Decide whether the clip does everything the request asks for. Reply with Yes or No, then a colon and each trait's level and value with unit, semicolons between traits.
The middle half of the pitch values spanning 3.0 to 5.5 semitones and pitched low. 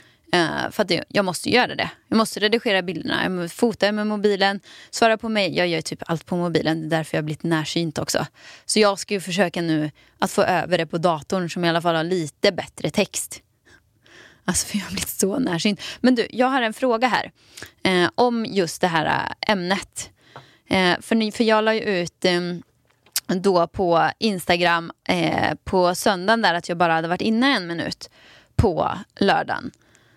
No: average, 4.1 semitones; medium, 180 Hz